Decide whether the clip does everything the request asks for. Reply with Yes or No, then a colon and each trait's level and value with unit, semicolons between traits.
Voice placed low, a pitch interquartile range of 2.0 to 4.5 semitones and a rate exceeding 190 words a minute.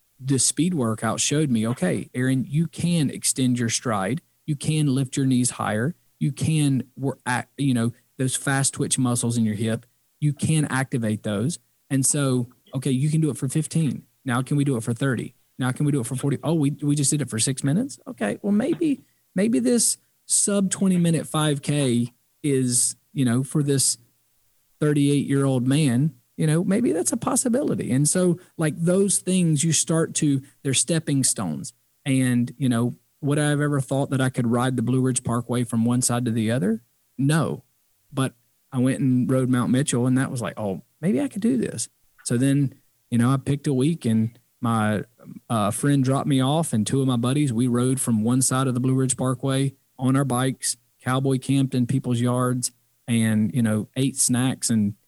Yes: low, 130 Hz; average, 3.2 semitones; average, 200 wpm